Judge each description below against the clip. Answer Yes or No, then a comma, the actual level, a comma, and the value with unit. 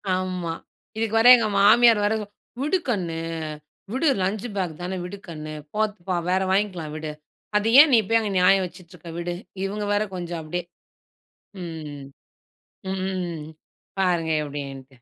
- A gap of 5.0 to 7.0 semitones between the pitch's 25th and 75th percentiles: No, average, 4.0 semitones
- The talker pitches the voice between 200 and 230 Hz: No, medium, 185 Hz